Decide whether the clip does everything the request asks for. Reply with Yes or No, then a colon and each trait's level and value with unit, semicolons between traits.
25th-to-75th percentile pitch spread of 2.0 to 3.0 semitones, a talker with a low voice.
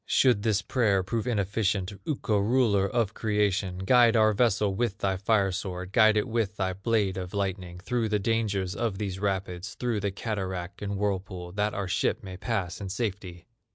Yes: narrow, 2.6 semitones; low, 100 Hz